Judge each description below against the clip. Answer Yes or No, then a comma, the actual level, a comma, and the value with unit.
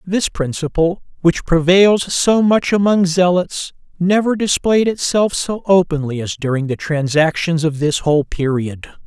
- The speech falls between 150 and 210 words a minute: No, average, 140 wpm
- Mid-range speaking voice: Yes, medium, 170 Hz